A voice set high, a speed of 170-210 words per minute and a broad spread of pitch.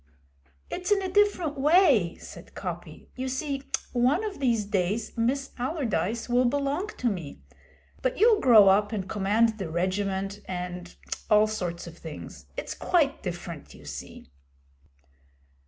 No: high, 225 Hz; average, 140 wpm; wide, 7.0 semitones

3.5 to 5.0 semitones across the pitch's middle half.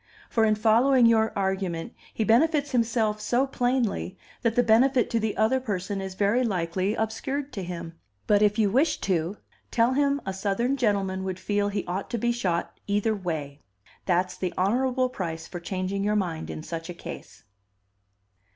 Yes: average, 4.2 semitones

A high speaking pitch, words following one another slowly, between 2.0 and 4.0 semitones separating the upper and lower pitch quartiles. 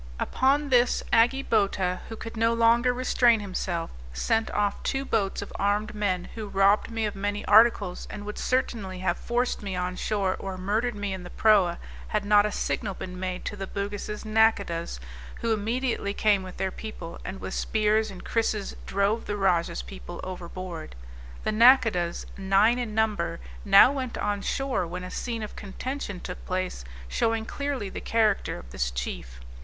No: high, 205 Hz; average, 175 wpm; average, 3.3 semitones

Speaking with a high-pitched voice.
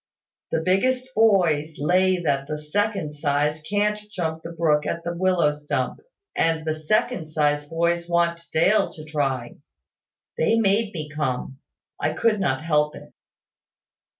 No: medium, 160 Hz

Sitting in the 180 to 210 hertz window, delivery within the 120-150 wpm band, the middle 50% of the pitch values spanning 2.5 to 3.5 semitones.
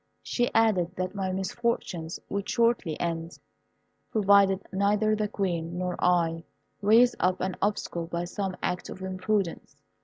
Yes: high, 190 Hz; average, 140 wpm; average, 2.9 semitones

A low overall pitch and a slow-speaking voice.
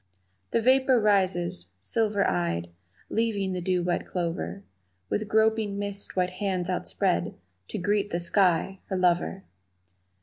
No: high, 190 Hz; slow, 130 wpm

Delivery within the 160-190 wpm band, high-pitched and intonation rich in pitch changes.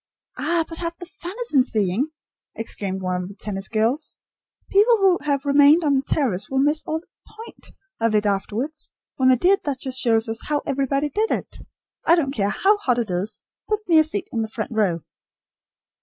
No: average, 200 wpm; very high, 275 Hz; wide, 6.6 semitones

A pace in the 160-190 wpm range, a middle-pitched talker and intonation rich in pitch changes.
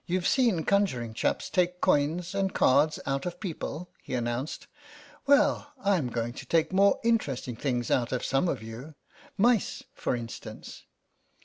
No: average, 150 wpm; medium, 155 Hz; wide, 7.4 semitones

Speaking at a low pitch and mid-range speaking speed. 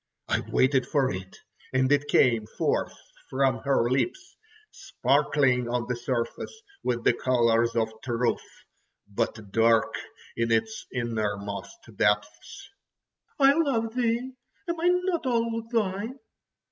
No: low, 130 Hz; slow, 120 wpm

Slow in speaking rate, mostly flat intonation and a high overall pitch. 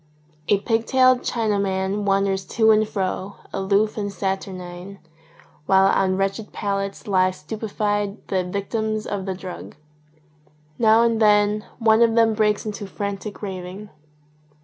Yes: slow, 130 wpm; narrow, 2.0 semitones; high, 200 Hz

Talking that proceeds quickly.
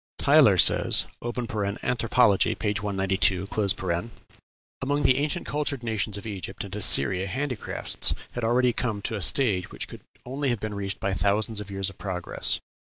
No: average, 150 wpm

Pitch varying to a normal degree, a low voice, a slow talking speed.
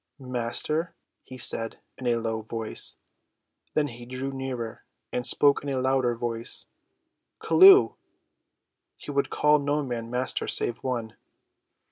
Yes: average, 3.1 semitones; low, 130 Hz; slow, 130 wpm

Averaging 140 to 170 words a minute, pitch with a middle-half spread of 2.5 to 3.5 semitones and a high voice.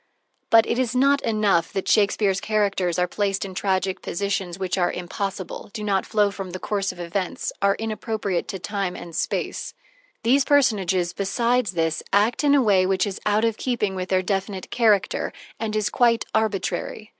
No: average, 180 wpm; average, 2.8 semitones; high, 200 Hz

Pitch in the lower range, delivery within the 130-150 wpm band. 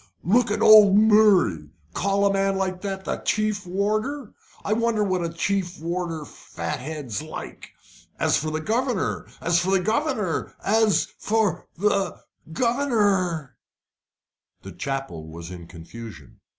No: high, 190 Hz; slow, 135 wpm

